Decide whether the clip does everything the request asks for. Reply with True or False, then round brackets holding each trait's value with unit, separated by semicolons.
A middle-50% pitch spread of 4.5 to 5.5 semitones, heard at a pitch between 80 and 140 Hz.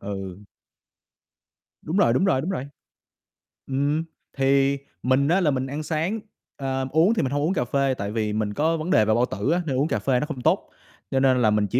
False (4.1 semitones; 135 Hz)